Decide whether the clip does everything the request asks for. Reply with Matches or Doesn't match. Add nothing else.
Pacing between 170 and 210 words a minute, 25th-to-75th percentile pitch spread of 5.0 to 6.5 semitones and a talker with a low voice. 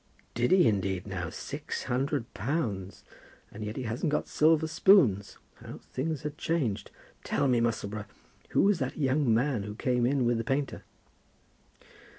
Doesn't match